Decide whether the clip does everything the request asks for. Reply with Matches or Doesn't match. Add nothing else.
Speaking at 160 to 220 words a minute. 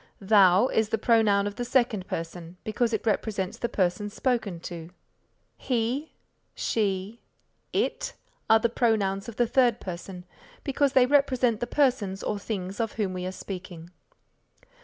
Doesn't match